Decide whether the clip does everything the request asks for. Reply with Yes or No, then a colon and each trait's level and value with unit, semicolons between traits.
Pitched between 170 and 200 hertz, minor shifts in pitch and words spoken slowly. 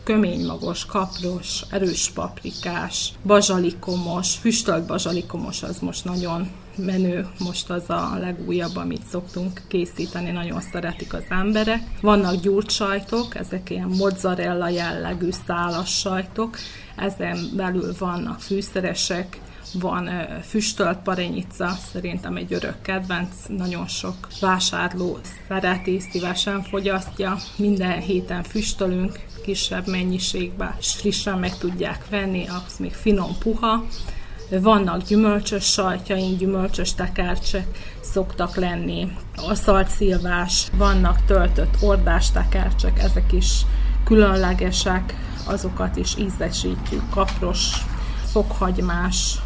Yes: medium, 185 Hz; narrow, 2.0 semitones; slow, 100 wpm